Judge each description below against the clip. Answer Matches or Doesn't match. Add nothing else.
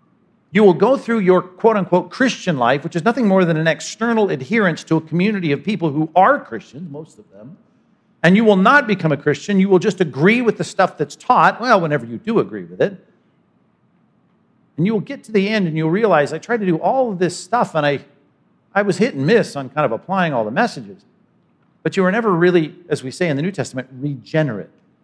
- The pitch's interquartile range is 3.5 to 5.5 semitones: Matches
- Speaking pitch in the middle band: Matches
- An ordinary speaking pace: Doesn't match